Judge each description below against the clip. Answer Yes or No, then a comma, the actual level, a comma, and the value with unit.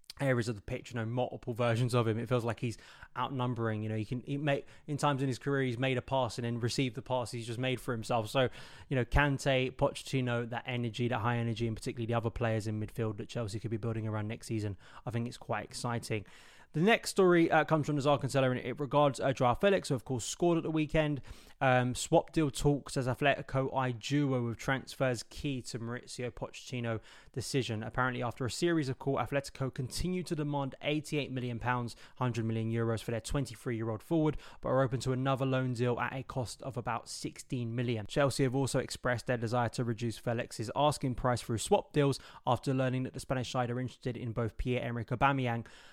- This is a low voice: Yes, low, 125 Hz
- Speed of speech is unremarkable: No, fast, 215 wpm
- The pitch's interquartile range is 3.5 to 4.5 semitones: No, average, 2.7 semitones